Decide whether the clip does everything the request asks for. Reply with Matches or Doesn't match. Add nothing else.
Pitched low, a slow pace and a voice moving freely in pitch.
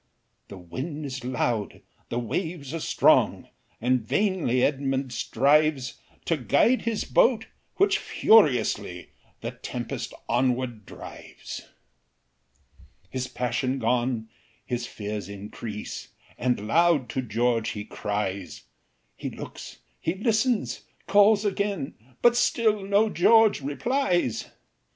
Matches